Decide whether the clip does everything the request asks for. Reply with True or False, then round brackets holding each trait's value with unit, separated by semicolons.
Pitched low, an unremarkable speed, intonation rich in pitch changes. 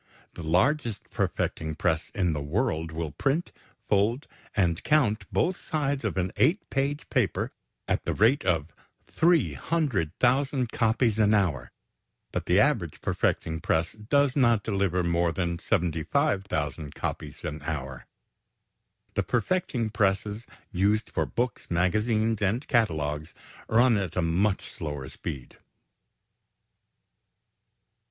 False (100 Hz; 120 wpm; 7.0 semitones)